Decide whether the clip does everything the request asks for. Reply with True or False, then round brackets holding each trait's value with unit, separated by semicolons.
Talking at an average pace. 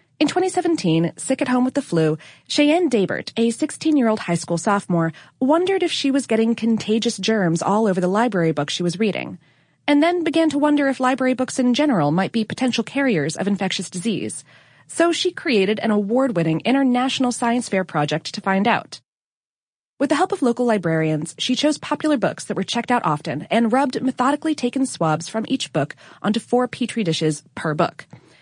True (185 wpm)